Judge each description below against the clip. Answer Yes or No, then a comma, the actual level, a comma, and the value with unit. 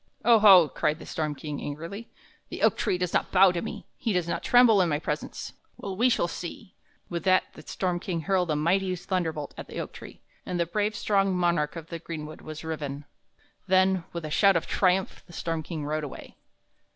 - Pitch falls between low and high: Yes, medium, 175 Hz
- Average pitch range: Yes, average, 3.4 semitones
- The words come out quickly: Yes, fast, 210 wpm